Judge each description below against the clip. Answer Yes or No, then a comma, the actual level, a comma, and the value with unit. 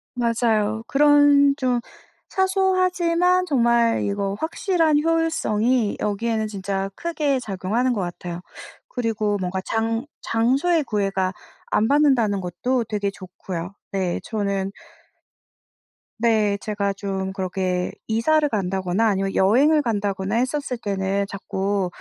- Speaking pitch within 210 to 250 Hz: Yes, high, 220 Hz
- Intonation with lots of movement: Yes, wide, 5.8 semitones